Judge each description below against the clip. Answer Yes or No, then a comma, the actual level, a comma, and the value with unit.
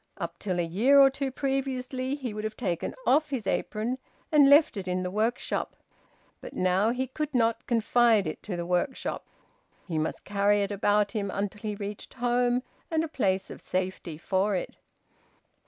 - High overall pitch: Yes, high, 215 Hz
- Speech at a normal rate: Yes, average, 180 wpm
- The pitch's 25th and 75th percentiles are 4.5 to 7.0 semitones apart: Yes, average, 5.2 semitones